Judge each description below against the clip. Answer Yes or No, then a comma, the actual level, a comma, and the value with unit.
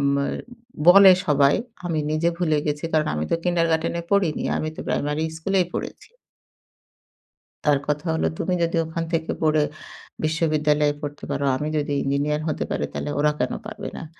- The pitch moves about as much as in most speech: No, narrow, 2.1 semitones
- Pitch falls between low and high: Yes, medium, 155 Hz